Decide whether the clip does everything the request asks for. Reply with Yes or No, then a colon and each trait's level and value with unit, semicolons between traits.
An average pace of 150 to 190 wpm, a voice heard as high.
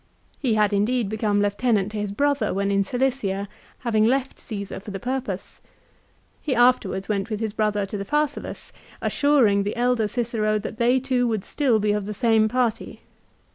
Yes: average, 180 wpm; high, 220 Hz